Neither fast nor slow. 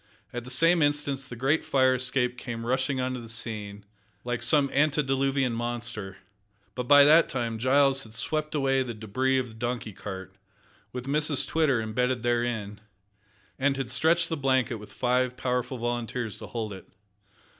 Yes: average, 165 wpm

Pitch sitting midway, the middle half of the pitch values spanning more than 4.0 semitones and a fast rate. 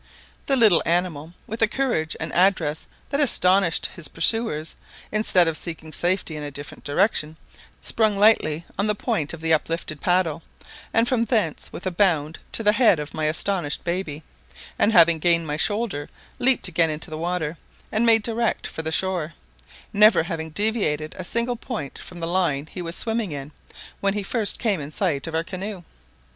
No: medium, 175 Hz; average, 5.1 semitones; average, 180 wpm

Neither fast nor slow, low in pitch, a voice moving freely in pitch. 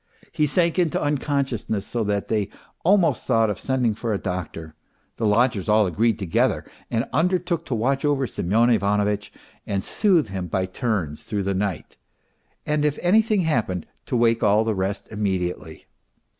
Yes: average, 160 wpm; low, 110 Hz; wide, 6.1 semitones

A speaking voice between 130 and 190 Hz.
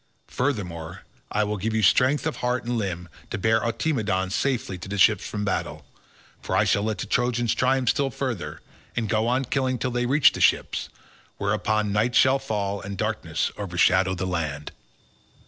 No: low, 110 Hz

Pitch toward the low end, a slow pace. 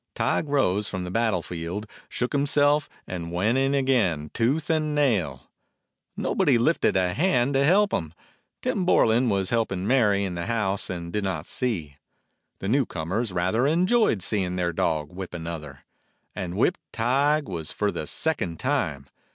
No: low, 105 Hz; average, 165 wpm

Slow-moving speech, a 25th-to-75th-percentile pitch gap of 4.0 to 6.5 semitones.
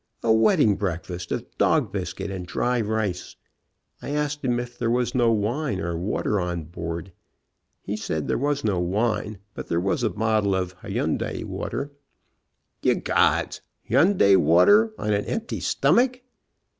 No: average, 155 wpm; average, 5.2 semitones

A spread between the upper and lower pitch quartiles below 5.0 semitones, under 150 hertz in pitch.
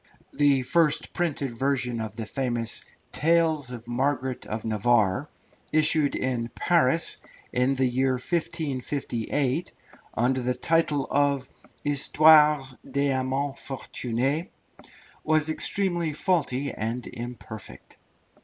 Yes: average, 3.5 semitones; low, 135 Hz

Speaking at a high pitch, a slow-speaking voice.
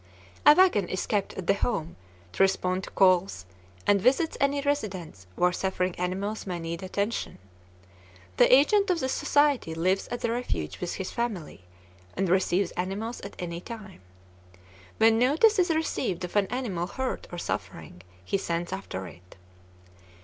No: high, 195 Hz; average, 155 wpm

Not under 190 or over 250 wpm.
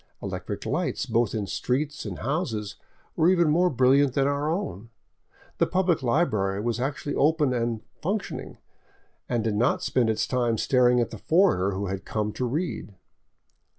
No: average, 165 wpm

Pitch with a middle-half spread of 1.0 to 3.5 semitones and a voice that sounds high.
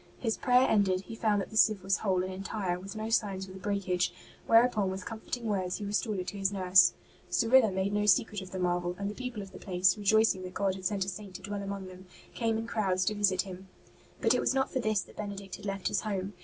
Yes: narrow, 2.5 semitones; high, 200 Hz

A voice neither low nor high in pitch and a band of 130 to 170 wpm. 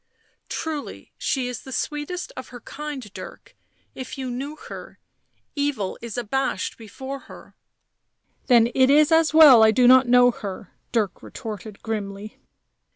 No: very high, 255 Hz; average, 160 wpm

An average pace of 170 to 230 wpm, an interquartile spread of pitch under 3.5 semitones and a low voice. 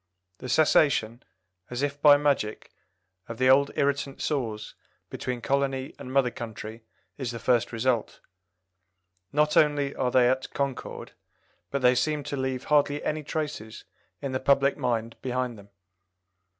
No: average, 145 wpm; average, 2.7 semitones; low, 130 Hz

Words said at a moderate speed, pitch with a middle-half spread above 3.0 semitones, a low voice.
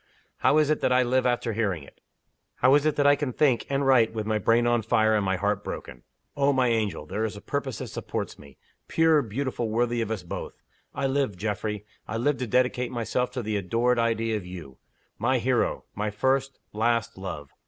No: fast, 215 wpm; average, 3.8 semitones; low, 115 Hz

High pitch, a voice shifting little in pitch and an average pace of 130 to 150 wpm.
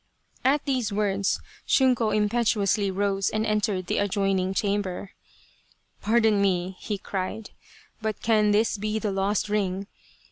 Yes: high, 205 Hz; narrow, 2.0 semitones; average, 145 wpm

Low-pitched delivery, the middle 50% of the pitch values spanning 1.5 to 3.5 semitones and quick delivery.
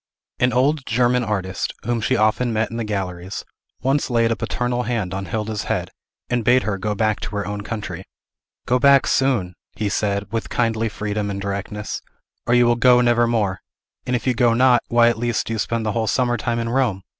Yes: low, 115 Hz; average, 2.8 semitones; fast, 215 wpm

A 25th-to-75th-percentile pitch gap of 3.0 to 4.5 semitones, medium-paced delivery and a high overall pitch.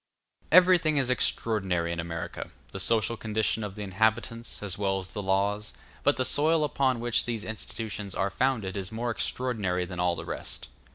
No: average, 4.1 semitones; average, 175 wpm; low, 110 Hz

